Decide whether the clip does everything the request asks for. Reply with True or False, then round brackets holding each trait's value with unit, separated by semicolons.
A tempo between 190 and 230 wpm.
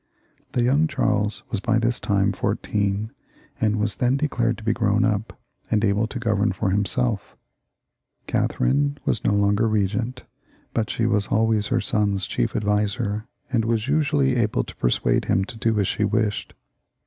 False (170 wpm)